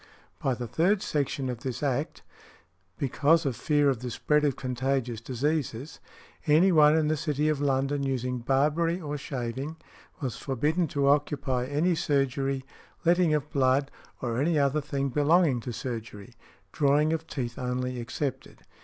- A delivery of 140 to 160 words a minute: Yes, average, 155 wpm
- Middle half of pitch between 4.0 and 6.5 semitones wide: No, average, 3.0 semitones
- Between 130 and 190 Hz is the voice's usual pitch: Yes, medium, 140 Hz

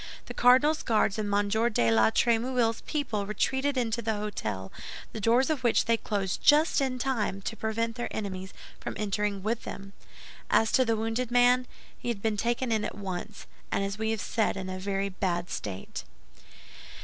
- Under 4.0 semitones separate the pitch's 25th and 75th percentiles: Yes, average, 3.4 semitones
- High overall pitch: Yes, high, 220 Hz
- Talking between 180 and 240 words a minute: Yes, average, 185 wpm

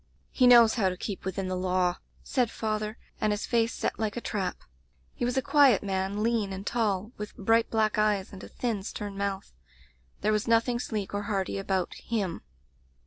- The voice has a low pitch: No, high, 210 Hz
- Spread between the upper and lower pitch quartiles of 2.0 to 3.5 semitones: Yes, average, 2.9 semitones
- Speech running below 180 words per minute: No, average, 195 wpm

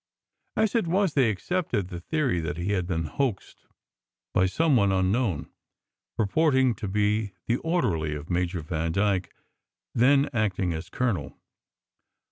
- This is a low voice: Yes, low, 100 Hz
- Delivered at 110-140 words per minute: Yes, slow, 135 wpm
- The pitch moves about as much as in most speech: No, wide, 6.9 semitones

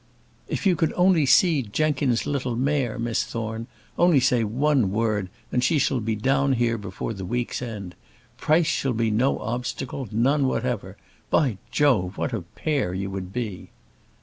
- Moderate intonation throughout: Yes, average, 4.4 semitones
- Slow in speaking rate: No, average, 165 wpm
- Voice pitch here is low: Yes, low, 120 Hz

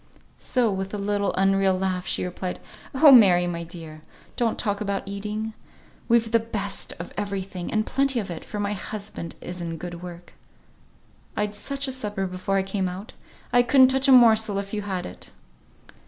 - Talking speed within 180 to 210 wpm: Yes, average, 185 wpm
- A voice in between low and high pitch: No, high, 200 Hz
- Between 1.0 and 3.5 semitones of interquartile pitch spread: Yes, average, 3.2 semitones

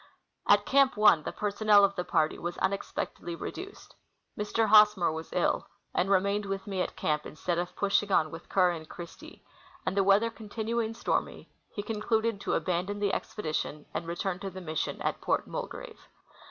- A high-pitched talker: Yes, high, 195 Hz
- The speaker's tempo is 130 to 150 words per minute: No, average, 180 wpm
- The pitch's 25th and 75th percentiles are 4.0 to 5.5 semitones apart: No, average, 3.3 semitones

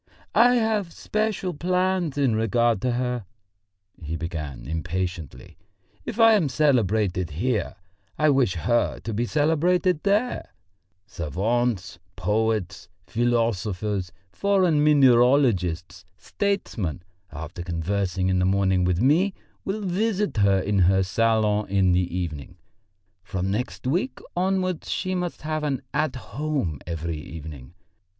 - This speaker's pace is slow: Yes, slow, 115 wpm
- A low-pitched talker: Yes, low, 110 Hz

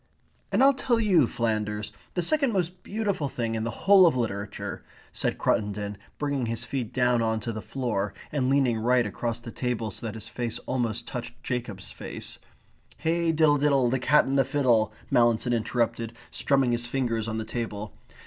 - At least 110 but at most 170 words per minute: No, average, 180 wpm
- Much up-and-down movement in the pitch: No, average, 3.9 semitones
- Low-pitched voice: Yes, low, 120 Hz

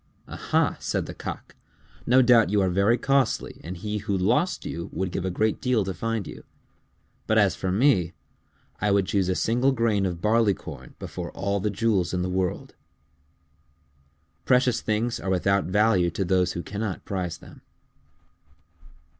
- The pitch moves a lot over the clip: No, average, 3.6 semitones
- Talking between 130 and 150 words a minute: No, average, 165 wpm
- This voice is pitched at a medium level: No, low, 100 Hz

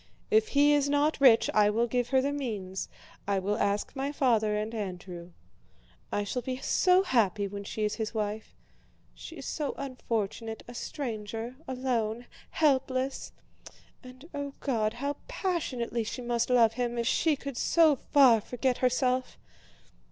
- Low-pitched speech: No, high, 245 Hz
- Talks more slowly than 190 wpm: Yes, average, 155 wpm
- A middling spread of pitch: Yes, average, 4.2 semitones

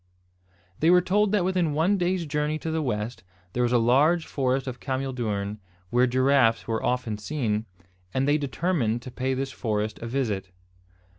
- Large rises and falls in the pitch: No, average, 5.0 semitones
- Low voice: Yes, low, 130 Hz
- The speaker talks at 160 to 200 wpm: Yes, average, 175 wpm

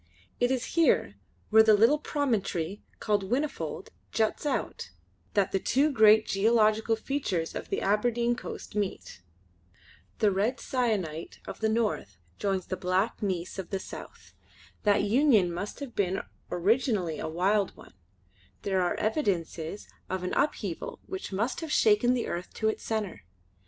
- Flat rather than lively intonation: No, average, 4.1 semitones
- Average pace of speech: Yes, average, 150 wpm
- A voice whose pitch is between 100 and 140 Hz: No, high, 210 Hz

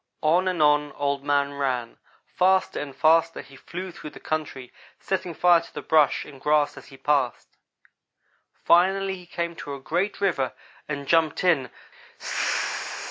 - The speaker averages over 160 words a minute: No, average, 155 wpm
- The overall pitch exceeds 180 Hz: No, medium, 155 Hz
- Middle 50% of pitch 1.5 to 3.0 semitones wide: No, average, 3.7 semitones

